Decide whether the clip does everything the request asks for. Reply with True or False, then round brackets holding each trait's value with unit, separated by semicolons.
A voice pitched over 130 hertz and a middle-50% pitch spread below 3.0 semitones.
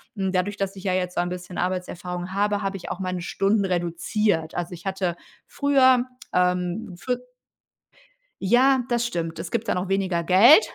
True (185 Hz; 2.6 semitones)